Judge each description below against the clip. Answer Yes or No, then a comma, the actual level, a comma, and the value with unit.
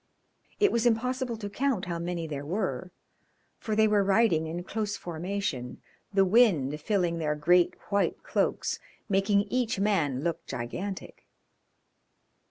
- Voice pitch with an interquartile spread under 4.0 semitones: No, average, 4.4 semitones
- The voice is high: Yes, high, 195 Hz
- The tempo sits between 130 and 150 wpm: Yes, slow, 135 wpm